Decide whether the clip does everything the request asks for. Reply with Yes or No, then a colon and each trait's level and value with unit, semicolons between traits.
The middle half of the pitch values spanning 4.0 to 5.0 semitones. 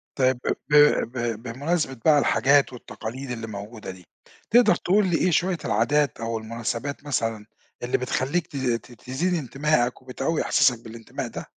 Yes: average, 4.3 semitones